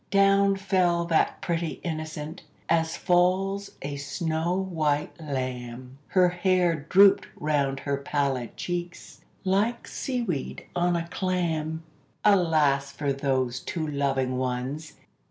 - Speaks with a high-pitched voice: No, medium, 160 Hz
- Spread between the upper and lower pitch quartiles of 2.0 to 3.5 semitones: No, average, 4.5 semitones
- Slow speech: Yes, slow, 120 wpm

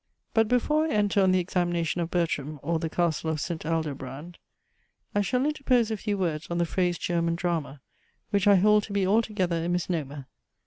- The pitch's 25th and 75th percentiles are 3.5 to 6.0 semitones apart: Yes, average, 3.9 semitones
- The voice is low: No, medium, 175 Hz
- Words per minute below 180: No, average, 190 wpm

